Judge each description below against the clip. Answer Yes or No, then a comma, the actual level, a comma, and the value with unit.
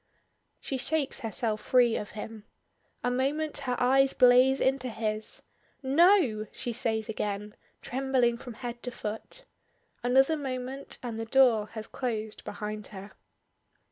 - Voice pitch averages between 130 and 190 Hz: No, high, 245 Hz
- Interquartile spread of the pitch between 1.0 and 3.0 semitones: No, average, 3.4 semitones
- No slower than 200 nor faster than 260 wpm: No, average, 140 wpm